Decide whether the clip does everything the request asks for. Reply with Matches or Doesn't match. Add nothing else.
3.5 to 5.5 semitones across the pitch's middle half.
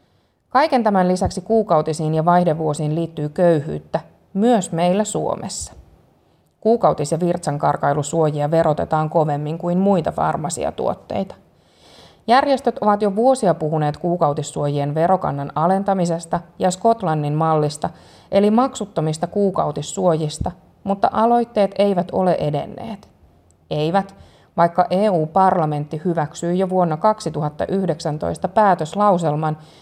Matches